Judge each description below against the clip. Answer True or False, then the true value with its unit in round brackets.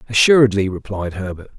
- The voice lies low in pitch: True (105 Hz)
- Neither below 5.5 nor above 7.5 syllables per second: True (6.0 syllables/s)